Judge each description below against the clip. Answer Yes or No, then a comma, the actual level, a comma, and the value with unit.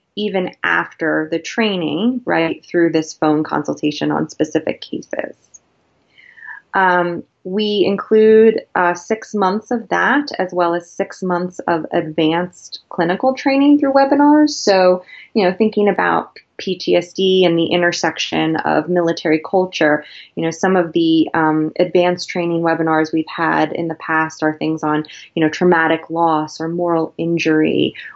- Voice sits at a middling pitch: Yes, medium, 175 Hz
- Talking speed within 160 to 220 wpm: No, average, 145 wpm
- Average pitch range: Yes, average, 3.7 semitones